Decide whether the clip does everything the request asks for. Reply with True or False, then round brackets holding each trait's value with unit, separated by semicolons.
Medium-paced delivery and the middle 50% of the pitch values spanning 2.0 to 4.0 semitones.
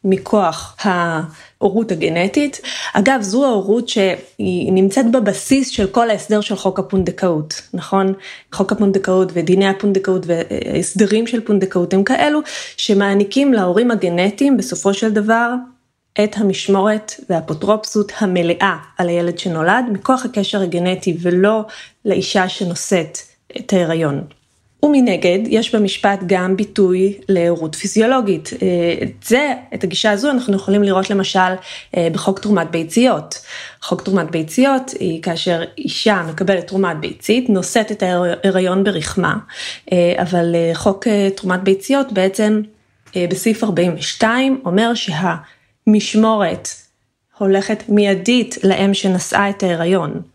True (110 wpm; 3.0 semitones)